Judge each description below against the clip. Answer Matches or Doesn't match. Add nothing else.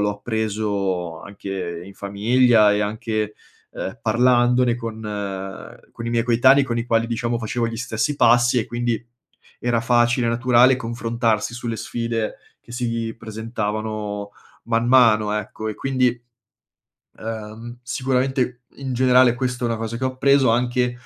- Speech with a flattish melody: Matches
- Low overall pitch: Matches